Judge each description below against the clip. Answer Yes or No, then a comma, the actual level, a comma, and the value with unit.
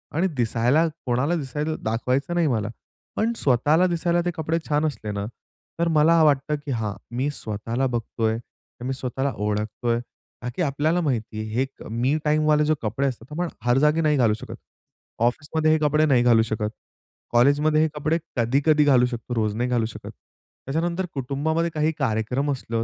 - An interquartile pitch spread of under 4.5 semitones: No, average, 4.8 semitones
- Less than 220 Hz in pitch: Yes, low, 135 Hz